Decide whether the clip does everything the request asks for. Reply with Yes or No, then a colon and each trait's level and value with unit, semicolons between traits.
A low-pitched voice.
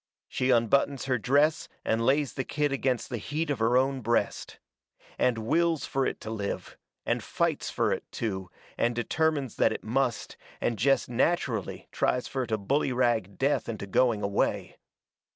Yes: low, 125 Hz